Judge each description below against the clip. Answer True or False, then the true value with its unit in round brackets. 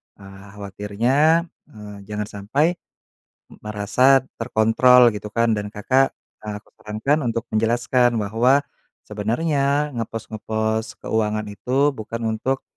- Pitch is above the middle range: False (115 Hz)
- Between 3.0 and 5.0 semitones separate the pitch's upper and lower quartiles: True (3.6 semitones)